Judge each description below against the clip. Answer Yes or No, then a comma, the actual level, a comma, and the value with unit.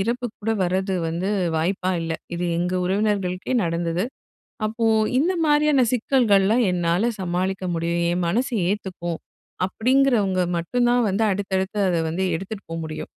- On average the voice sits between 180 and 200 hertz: Yes, high, 190 Hz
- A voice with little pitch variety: No, average, 4.7 semitones